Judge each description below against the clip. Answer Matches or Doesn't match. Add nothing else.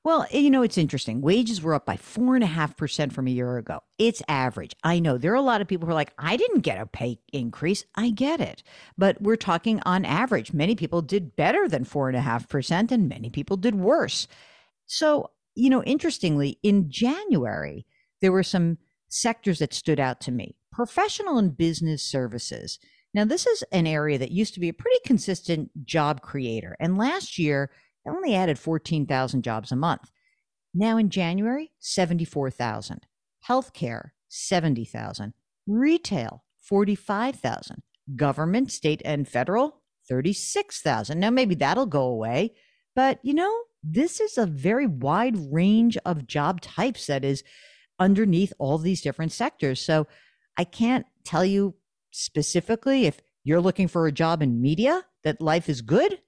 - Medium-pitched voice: Matches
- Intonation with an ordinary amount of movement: Doesn't match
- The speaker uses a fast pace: Doesn't match